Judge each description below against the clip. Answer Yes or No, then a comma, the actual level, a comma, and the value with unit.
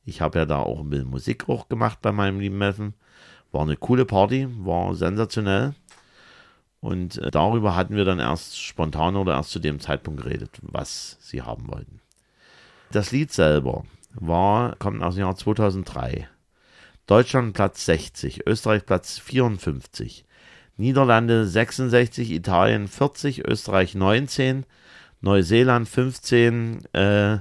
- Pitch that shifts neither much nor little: Yes, average, 4.7 semitones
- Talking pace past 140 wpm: No, average, 135 wpm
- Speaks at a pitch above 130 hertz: No, low, 100 Hz